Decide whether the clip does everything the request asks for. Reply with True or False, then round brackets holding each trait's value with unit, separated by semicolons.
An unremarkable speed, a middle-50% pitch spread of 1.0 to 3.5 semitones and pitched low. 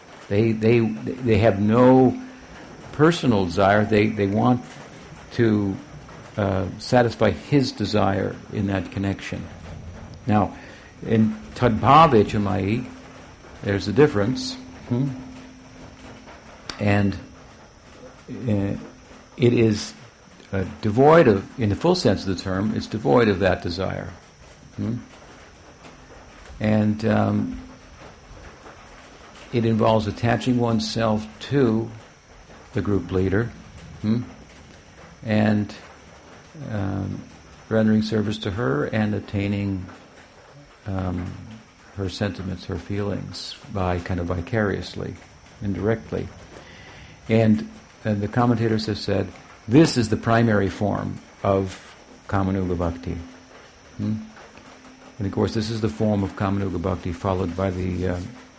False (105 wpm; 2.8 semitones; 105 Hz)